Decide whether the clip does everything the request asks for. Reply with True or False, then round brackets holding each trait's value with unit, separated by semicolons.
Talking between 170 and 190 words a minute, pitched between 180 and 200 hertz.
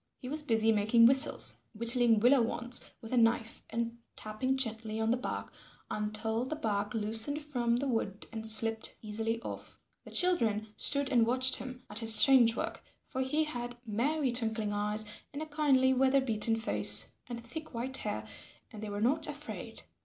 False (175 wpm; 235 Hz)